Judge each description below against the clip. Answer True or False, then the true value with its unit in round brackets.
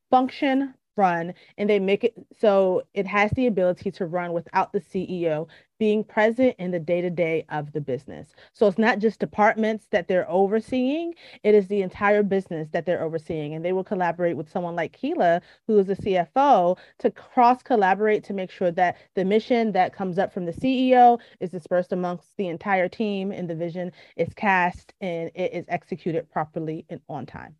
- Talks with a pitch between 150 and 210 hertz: True (190 Hz)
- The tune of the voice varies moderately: True (3.5 semitones)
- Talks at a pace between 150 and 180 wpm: False (190 wpm)